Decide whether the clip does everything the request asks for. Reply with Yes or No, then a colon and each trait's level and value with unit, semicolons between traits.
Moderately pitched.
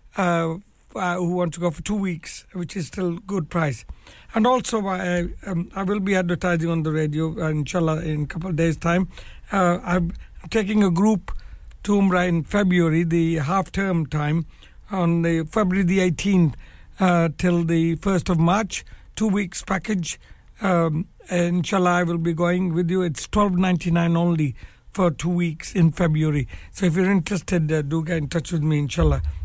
Yes: medium, 175 Hz